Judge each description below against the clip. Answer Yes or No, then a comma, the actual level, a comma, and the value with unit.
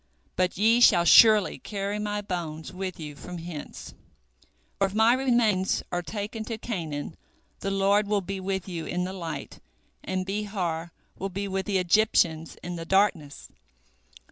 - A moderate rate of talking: Yes, average, 160 wpm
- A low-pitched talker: No, high, 190 Hz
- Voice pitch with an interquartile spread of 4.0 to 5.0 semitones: No, average, 3.1 semitones